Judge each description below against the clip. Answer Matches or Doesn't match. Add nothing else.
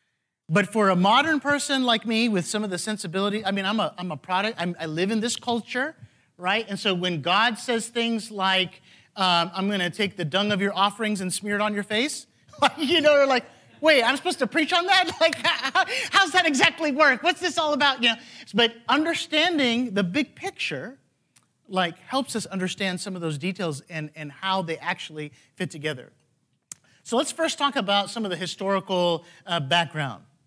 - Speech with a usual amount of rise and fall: Doesn't match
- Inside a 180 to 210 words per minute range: Matches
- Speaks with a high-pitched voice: Matches